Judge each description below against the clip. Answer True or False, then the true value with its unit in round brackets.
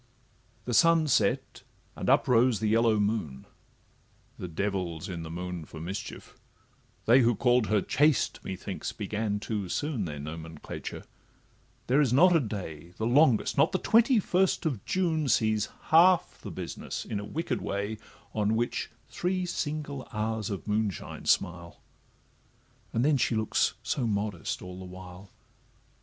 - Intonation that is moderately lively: False (6.6 semitones)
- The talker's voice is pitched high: False (110 Hz)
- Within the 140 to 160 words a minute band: True (150 wpm)